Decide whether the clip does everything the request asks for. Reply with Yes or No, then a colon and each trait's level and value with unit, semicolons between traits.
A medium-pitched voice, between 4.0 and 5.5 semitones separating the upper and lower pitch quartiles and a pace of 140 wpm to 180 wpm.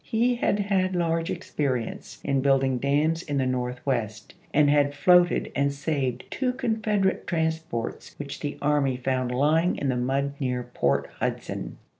Yes: medium, 145 Hz; average, 4.6 semitones; average, 150 wpm